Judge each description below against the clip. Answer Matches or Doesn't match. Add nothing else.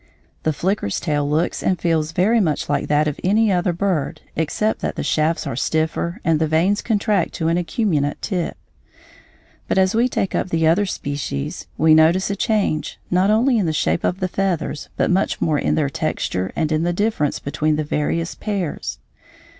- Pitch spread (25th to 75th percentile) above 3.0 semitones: Matches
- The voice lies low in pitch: Doesn't match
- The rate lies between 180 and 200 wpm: Matches